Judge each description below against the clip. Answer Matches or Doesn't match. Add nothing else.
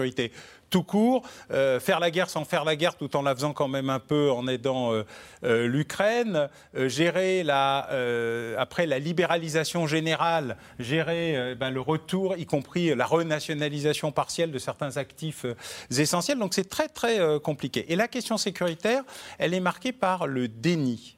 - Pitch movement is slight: Doesn't match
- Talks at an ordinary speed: Matches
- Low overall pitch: Doesn't match